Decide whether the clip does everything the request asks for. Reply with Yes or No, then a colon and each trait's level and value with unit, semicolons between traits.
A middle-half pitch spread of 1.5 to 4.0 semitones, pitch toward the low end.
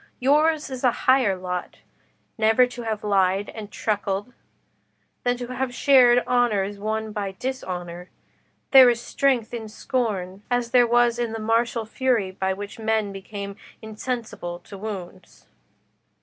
No: average, 3.6 semitones; high, 220 Hz